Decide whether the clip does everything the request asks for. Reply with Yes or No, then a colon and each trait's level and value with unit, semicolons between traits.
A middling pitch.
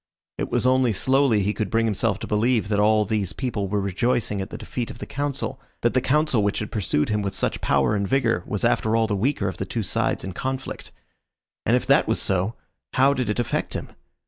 No: low, 110 Hz